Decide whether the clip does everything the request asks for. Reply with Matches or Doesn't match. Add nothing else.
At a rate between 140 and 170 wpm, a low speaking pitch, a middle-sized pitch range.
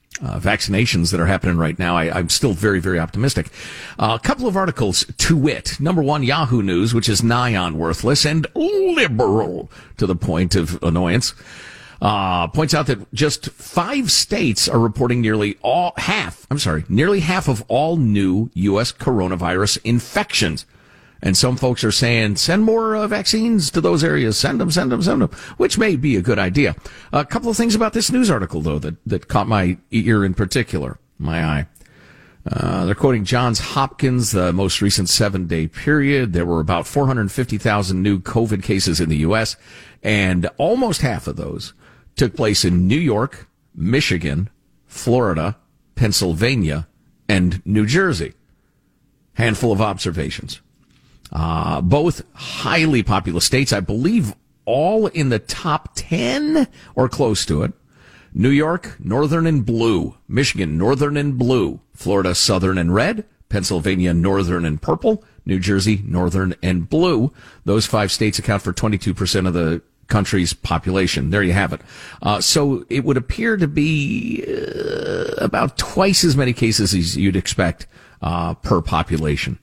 Doesn't match